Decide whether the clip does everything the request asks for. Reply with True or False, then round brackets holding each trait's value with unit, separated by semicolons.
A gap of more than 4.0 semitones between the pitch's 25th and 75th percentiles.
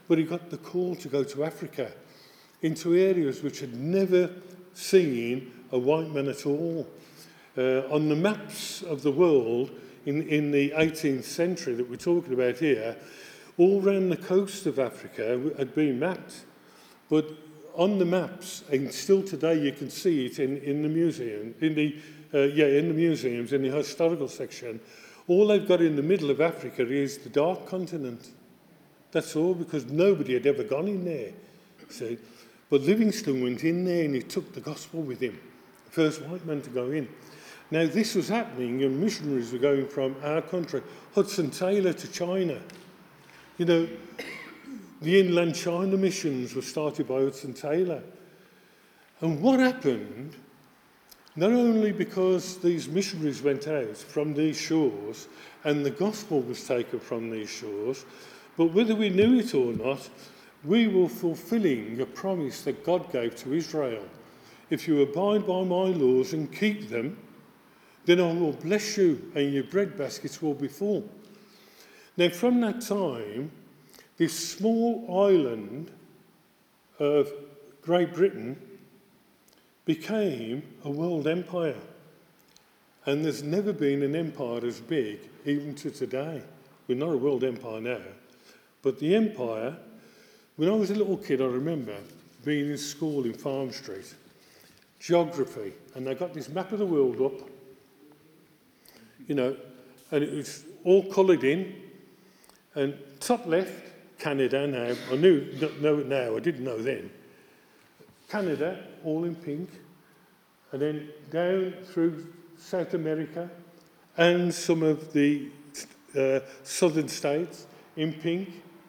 True (4.7 semitones)